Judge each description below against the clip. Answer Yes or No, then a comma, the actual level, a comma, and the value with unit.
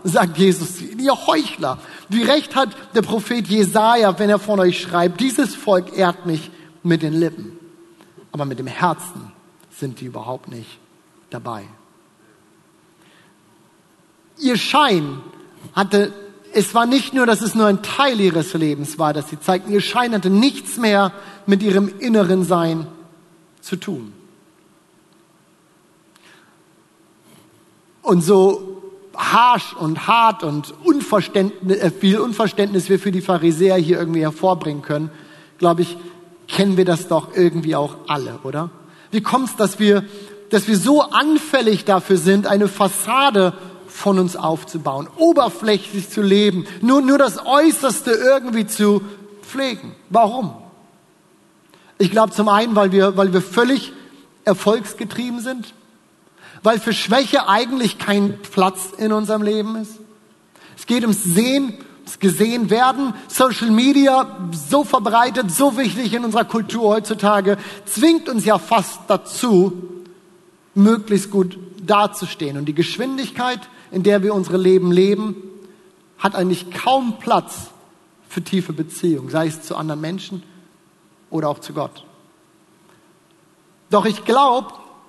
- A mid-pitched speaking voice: No, high, 195 Hz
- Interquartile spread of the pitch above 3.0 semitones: Yes, average, 4.0 semitones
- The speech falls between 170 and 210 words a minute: No, average, 130 wpm